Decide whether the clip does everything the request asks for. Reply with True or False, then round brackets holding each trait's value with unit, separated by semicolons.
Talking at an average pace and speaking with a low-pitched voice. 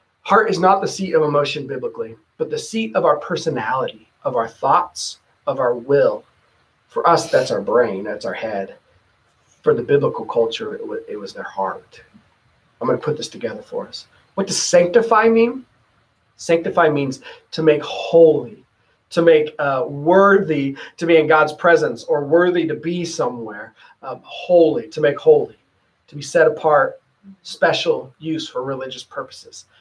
False (165 wpm; 175 Hz)